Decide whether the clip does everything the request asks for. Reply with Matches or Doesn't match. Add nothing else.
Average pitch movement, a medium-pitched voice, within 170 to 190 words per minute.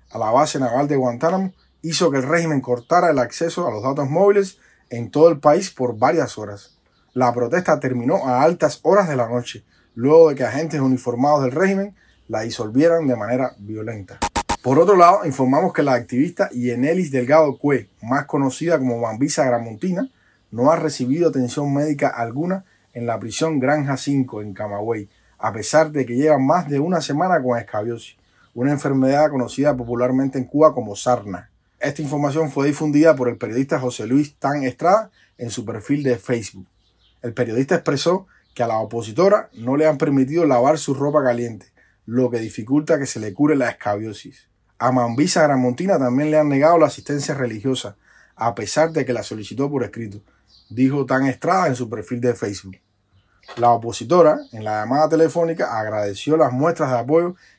Doesn't match